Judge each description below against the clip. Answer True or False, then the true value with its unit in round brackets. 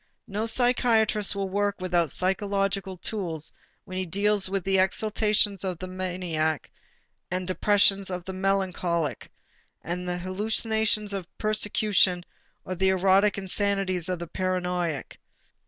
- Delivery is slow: True (130 wpm)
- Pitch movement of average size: False (2.2 semitones)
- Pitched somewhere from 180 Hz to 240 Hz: True (190 Hz)